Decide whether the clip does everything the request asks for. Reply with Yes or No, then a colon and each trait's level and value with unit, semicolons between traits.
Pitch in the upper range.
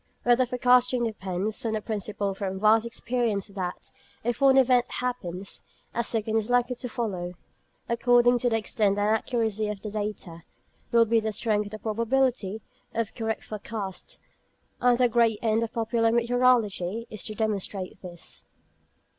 Yes: high, 220 Hz